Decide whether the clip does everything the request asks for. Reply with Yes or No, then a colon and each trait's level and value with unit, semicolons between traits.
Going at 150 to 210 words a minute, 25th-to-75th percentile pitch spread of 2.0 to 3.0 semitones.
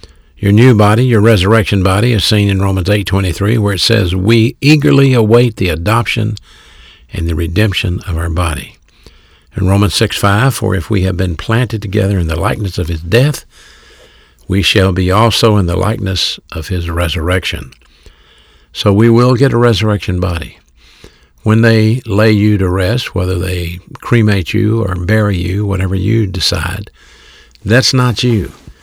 No: average, 160 wpm; average, 3.9 semitones